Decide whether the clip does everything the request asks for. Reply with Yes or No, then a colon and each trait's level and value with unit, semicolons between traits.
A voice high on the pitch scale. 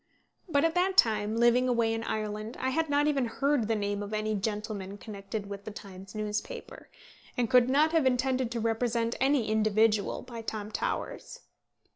Yes: high, 225 Hz